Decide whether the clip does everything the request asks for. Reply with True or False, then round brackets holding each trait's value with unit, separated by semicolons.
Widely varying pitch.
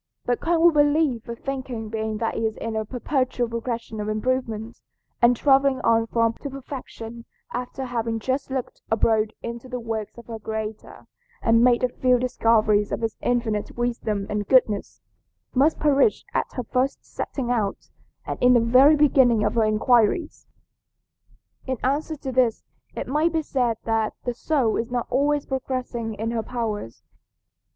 False (2.8 semitones)